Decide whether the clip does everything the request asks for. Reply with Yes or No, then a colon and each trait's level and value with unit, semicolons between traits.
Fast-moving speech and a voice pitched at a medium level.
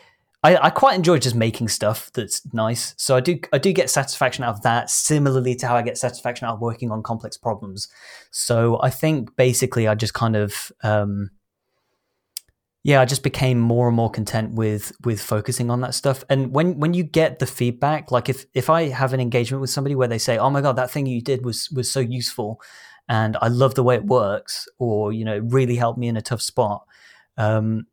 No: fast, 220 wpm; low, 125 Hz